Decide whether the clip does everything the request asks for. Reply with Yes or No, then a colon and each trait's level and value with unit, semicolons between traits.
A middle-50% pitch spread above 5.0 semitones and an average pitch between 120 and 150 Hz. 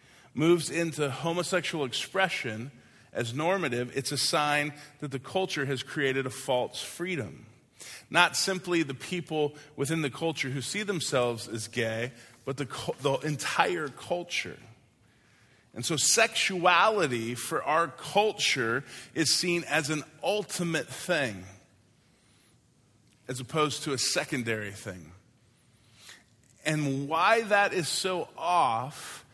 Yes: wide, 5.6 semitones; medium, 140 Hz